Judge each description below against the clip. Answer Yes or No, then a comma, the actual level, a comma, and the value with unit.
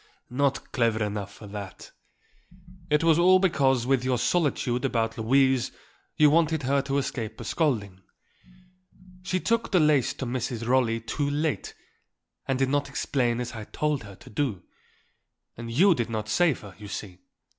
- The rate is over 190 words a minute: No, average, 165 wpm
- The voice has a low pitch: Yes, low, 130 Hz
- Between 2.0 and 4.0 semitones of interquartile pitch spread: No, average, 4.5 semitones